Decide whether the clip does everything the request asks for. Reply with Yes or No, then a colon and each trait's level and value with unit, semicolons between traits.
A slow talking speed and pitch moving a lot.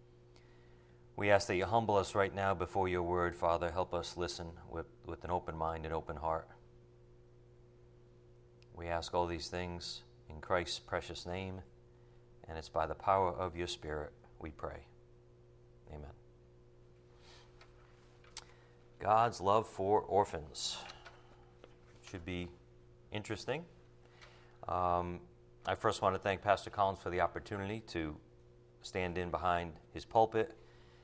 Yes: slow, 130 wpm; wide, 6.8 semitones